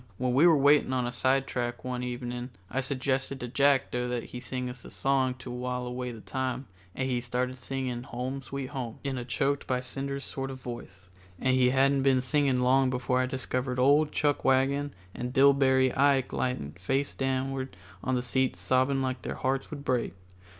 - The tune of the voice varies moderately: No, narrow, 1.4 semitones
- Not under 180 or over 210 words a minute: Yes, average, 190 wpm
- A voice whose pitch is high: No, low, 130 Hz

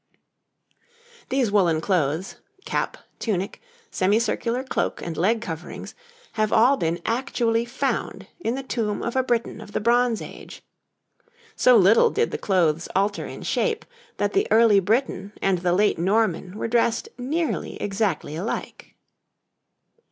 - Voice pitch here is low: No, high, 215 Hz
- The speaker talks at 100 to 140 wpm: Yes, slow, 135 wpm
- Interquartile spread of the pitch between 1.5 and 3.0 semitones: No, average, 4.3 semitones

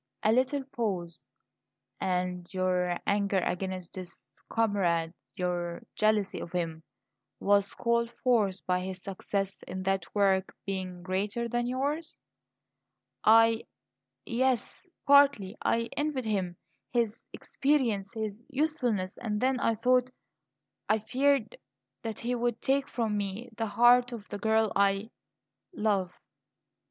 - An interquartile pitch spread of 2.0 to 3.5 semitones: No, average, 4.3 semitones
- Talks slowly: Yes, slow, 125 wpm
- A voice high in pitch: Yes, high, 210 Hz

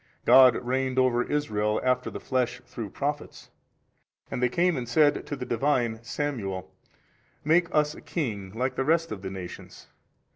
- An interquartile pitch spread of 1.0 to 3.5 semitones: No, average, 4.4 semitones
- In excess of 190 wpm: No, average, 160 wpm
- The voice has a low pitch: Yes, low, 125 Hz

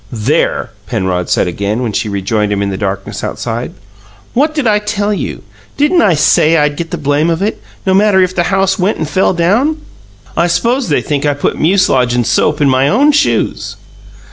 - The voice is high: No, medium, 170 Hz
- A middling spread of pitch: No, wide, 8.3 semitones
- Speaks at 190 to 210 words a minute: Yes, average, 200 wpm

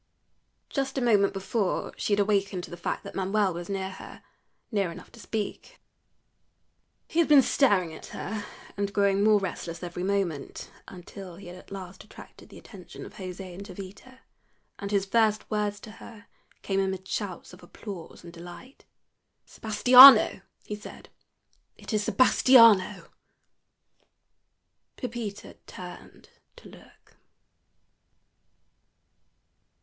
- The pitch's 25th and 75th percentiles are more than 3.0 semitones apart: No, narrow, 2.6 semitones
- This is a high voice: Yes, high, 200 Hz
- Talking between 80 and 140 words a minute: Yes, slow, 135 wpm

